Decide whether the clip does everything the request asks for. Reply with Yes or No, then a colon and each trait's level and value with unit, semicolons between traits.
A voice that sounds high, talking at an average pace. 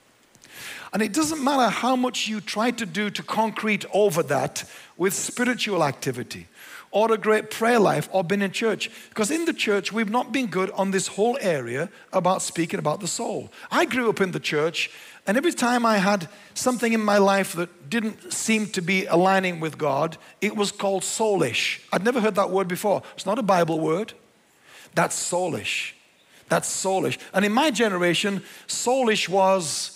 Yes: high, 205 Hz; average, 180 wpm